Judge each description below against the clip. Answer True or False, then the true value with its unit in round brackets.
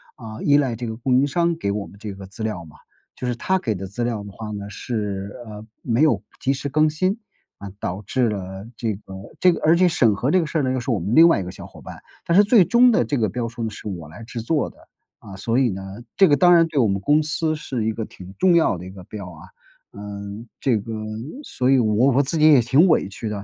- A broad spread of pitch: True (6.7 semitones)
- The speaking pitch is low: True (115 Hz)